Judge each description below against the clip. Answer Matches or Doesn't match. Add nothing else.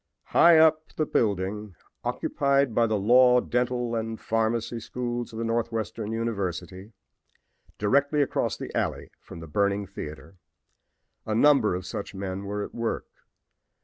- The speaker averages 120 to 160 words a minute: Matches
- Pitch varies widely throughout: Doesn't match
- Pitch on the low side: Matches